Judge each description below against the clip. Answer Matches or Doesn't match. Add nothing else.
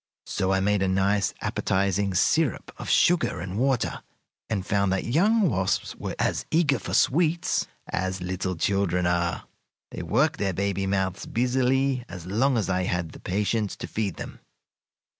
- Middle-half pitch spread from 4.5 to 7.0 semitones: Matches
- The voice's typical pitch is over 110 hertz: Doesn't match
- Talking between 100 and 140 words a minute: Doesn't match